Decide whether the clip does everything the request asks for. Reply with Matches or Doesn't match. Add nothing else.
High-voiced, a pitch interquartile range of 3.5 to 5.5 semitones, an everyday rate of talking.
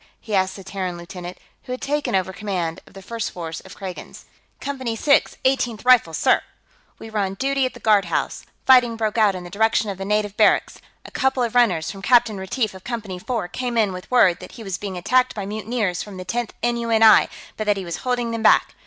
Doesn't match